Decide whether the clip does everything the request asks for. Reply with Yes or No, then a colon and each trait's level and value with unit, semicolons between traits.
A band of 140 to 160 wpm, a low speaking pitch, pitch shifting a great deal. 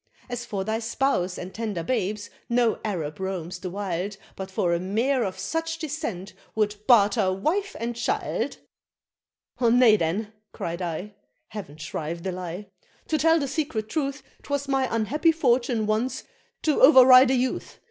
No: average, 155 wpm; high, 220 Hz; wide, 5.8 semitones